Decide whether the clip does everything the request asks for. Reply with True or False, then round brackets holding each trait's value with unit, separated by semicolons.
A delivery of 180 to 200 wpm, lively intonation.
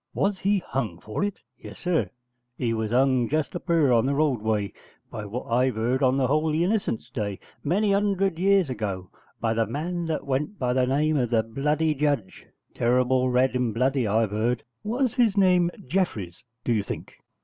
True (185 wpm; 6.6 semitones)